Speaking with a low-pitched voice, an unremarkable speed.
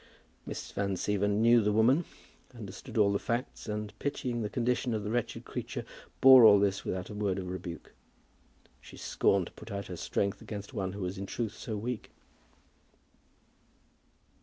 Yes: low, 105 Hz; average, 170 wpm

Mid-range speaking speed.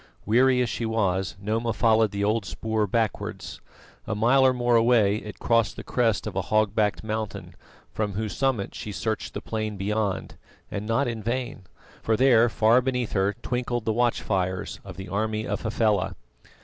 Yes: average, 180 wpm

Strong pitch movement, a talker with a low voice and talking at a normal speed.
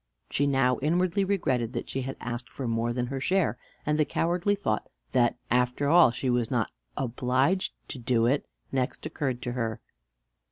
No: average, 3.8 semitones; low, 130 Hz; average, 175 wpm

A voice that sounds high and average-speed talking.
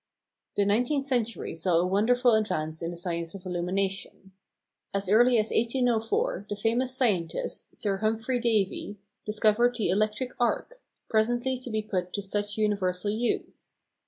Yes: high, 215 Hz; average, 145 wpm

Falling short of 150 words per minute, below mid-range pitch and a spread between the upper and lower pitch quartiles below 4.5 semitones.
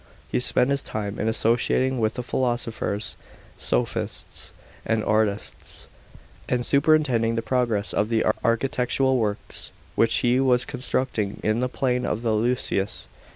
Yes: slow, 135 wpm; low, 120 Hz; narrow, 2.6 semitones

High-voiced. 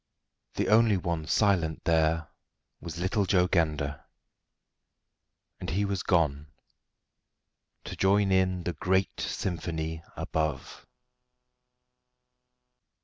No: very low, 85 Hz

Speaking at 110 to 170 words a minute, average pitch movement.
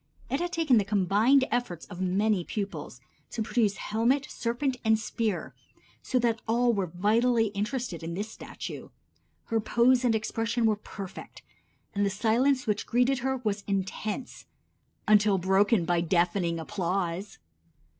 Yes: average, 145 wpm; average, 3.7 semitones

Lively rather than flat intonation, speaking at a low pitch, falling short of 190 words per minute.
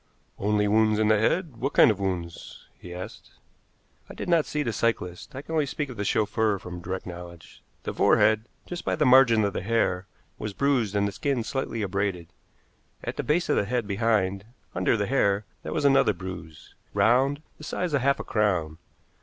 No: wide, 5.7 semitones; low, 110 Hz; average, 200 wpm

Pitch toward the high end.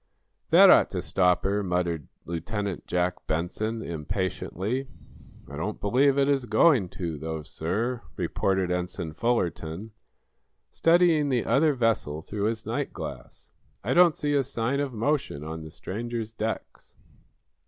No: low, 105 Hz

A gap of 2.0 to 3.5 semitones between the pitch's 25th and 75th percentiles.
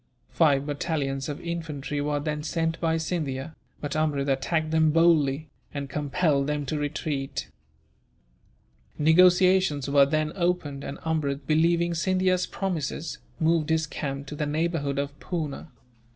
Yes: narrow, 2.6 semitones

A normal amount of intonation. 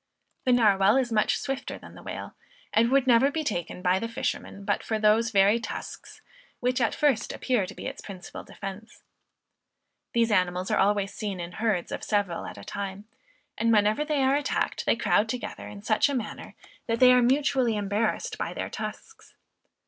Yes: average, 3.8 semitones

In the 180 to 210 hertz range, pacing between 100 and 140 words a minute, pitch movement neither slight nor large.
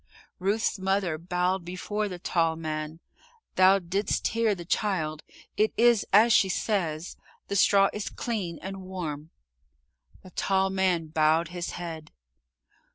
Yes: medium, 185 Hz; slow, 135 wpm; average, 3.1 semitones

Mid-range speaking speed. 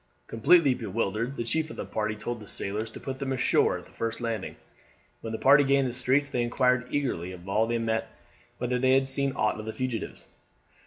No: fast, 215 wpm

